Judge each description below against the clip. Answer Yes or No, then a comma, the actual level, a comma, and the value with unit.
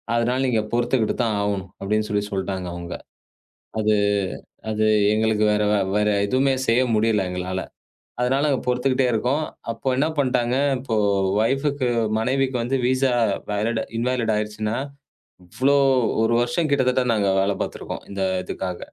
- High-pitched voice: No, low, 115 Hz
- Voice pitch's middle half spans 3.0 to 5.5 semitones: Yes, average, 3.5 semitones